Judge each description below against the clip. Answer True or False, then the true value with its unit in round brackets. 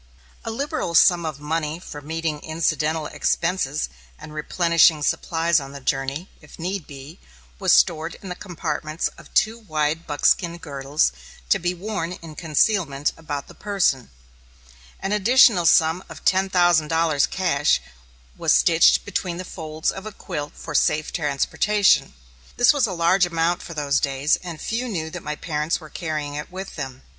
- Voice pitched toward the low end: False (165 Hz)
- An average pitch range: True (3.3 semitones)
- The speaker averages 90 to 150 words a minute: False (165 wpm)